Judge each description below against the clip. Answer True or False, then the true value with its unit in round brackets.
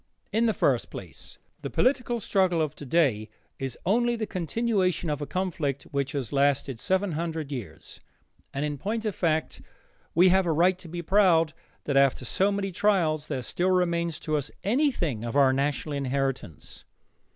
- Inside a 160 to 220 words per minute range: True (170 wpm)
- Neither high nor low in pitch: True (165 Hz)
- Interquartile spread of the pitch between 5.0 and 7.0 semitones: True (5.3 semitones)